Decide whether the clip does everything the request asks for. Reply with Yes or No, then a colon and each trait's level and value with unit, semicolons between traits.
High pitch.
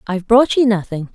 Yes: high, 215 Hz